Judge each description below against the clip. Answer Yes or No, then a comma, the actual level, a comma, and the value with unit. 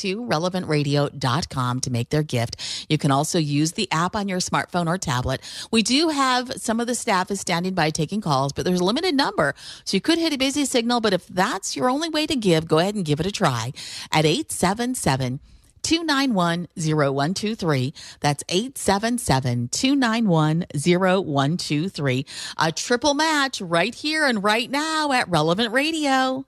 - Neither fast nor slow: Yes, average, 165 wpm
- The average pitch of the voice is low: No, medium, 180 Hz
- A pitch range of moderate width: No, wide, 8.2 semitones